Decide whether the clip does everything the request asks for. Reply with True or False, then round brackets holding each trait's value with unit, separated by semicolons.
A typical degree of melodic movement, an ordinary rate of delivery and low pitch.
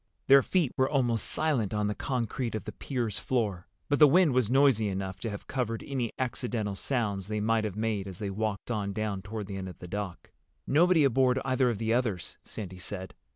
False (4.3 semitones; 210 wpm; 110 Hz)